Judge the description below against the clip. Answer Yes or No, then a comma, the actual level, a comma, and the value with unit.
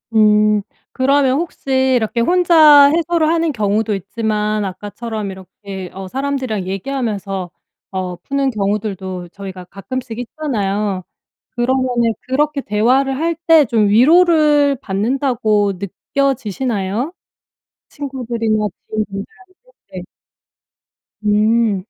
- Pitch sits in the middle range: No, high, 230 Hz